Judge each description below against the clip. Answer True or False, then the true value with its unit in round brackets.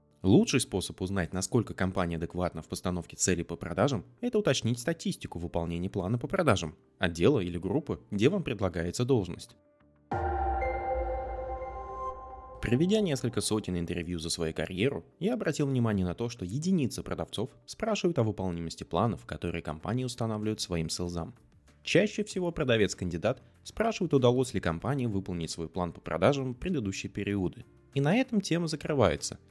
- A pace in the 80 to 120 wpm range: False (140 wpm)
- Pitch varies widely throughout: True (8.8 semitones)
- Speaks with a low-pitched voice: True (105 Hz)